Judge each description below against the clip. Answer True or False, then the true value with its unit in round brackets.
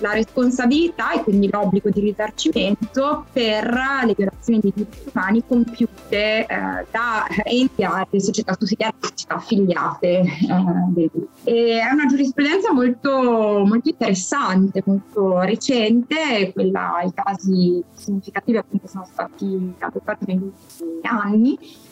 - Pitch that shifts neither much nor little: True (4.1 semitones)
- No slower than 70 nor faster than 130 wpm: True (120 wpm)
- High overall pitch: True (215 Hz)